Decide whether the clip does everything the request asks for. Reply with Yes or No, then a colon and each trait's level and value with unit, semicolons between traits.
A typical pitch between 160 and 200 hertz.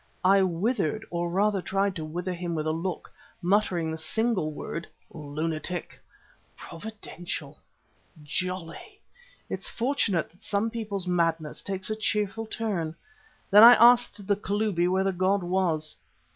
Yes: medium, 185 Hz